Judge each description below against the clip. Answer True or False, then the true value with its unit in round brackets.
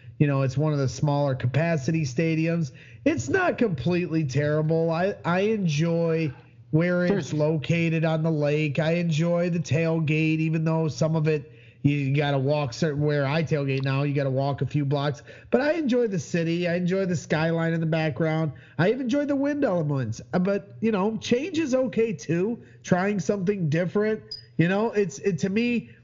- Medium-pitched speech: True (160 Hz)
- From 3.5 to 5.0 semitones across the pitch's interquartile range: True (3.9 semitones)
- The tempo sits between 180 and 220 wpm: True (185 wpm)